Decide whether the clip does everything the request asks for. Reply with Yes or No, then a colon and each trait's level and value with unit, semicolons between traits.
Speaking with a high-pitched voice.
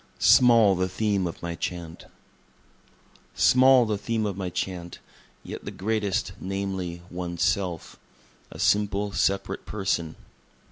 No: very low, 95 Hz